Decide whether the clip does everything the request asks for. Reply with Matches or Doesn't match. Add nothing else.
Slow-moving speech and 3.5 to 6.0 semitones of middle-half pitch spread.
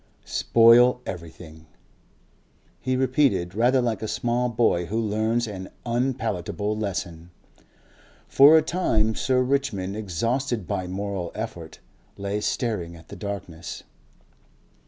Matches